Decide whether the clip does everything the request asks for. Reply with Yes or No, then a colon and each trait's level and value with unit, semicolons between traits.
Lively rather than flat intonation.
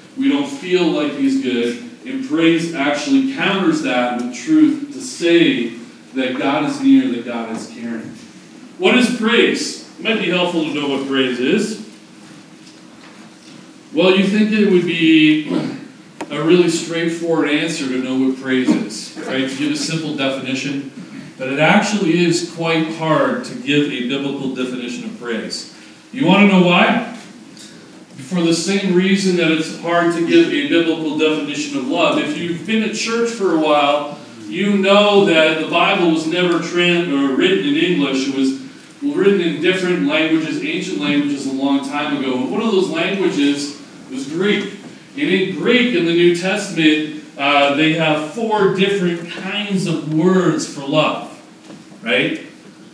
Yes: wide, 7.0 semitones